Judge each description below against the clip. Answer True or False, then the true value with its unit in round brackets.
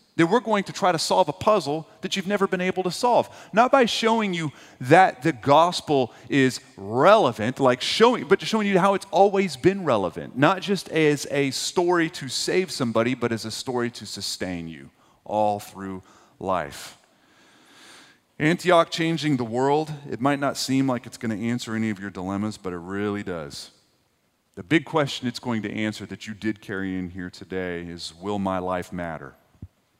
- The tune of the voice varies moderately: False (8.9 semitones)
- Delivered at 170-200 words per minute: True (190 wpm)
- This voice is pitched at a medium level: False (130 Hz)